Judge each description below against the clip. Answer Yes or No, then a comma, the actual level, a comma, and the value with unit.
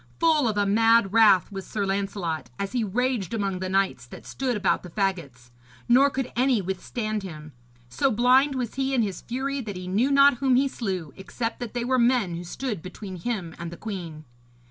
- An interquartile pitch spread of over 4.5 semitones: Yes, average, 5.1 semitones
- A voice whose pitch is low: No, high, 210 Hz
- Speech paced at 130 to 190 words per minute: No, fast, 205 wpm